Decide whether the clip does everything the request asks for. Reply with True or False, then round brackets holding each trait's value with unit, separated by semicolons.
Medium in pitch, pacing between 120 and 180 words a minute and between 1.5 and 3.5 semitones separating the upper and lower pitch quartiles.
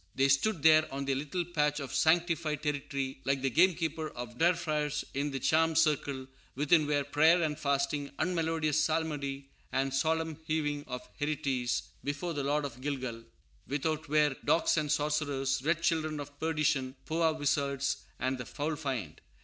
True (150 Hz; 160 wpm; 2.4 semitones)